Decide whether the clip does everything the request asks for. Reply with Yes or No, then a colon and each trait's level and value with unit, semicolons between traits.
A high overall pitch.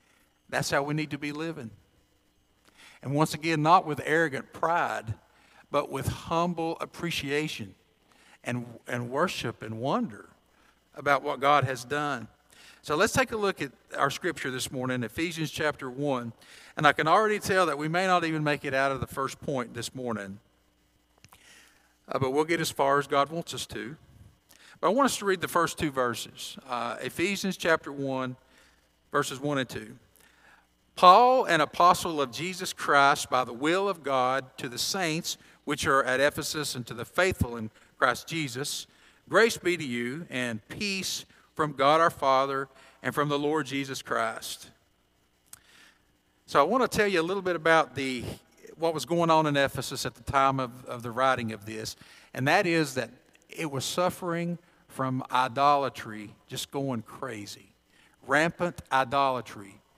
No: medium, 140 Hz